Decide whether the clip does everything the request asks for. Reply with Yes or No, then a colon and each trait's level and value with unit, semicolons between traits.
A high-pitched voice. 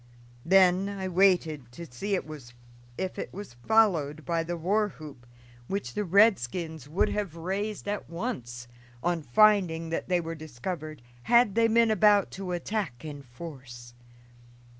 No: medium, 170 Hz